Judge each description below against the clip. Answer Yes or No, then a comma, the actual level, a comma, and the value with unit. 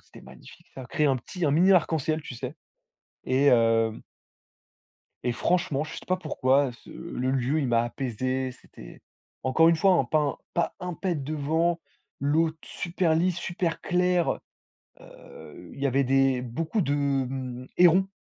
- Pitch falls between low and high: Yes, medium, 145 Hz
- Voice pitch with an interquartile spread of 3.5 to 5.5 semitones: Yes, average, 4.7 semitones